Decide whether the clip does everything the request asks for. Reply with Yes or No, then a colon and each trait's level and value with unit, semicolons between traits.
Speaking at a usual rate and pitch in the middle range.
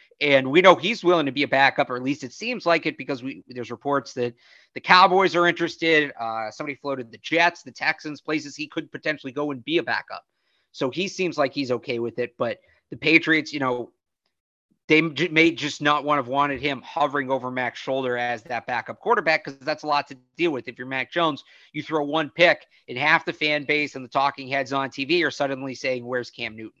No: fast, 230 wpm; medium, 145 Hz